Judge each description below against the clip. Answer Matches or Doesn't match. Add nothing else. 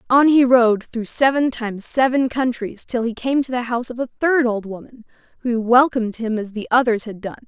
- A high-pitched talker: Matches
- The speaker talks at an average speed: Doesn't match